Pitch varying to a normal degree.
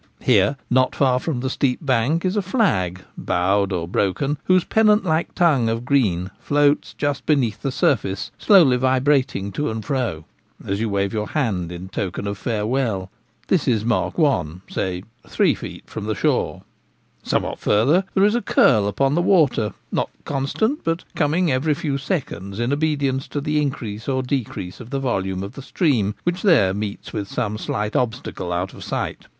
No: wide, 6.4 semitones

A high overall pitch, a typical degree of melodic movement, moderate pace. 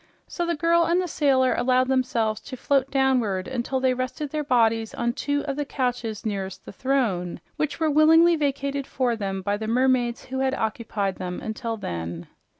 Yes: very high, 255 Hz; average, 4.1 semitones; average, 180 wpm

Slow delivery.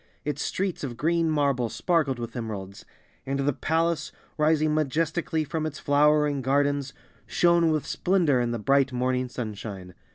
No: average, 150 wpm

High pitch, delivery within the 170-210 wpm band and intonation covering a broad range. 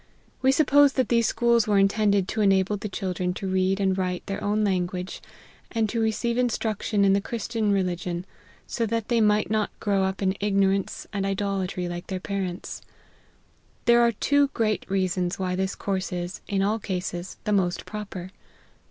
No: high, 200 Hz; average, 180 wpm; narrow, 2.6 semitones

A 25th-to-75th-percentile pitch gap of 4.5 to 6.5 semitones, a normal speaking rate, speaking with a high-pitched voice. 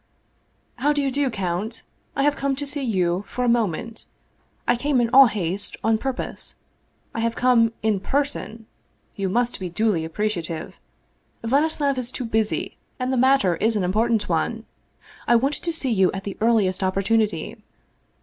Yes: average, 4.9 semitones; average, 170 wpm; high, 230 Hz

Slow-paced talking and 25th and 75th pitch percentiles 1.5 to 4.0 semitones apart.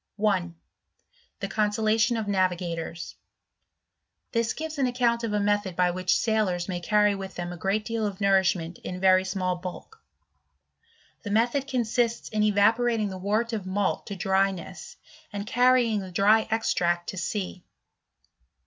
No: average, 150 wpm; average, 3.3 semitones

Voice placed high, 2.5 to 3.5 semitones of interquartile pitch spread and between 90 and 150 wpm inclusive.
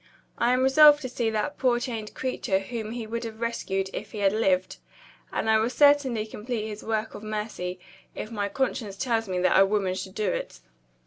No: high, 220 Hz; average, 3.1 semitones; fast, 205 wpm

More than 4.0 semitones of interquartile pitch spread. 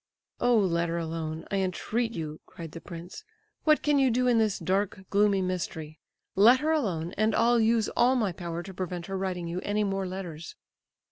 Yes: average, 4.8 semitones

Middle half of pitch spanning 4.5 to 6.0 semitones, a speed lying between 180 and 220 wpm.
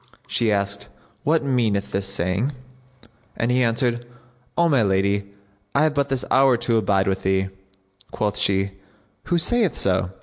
No: average, 5.3 semitones; average, 155 wpm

